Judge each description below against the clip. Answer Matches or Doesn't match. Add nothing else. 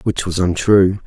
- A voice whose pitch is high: Doesn't match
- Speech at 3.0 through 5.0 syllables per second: Matches